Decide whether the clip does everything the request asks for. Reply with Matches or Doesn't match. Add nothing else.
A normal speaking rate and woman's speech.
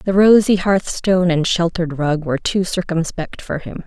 Matches